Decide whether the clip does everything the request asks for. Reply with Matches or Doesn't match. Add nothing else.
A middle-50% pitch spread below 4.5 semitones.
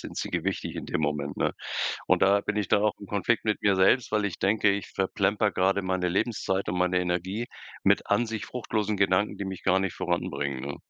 Matches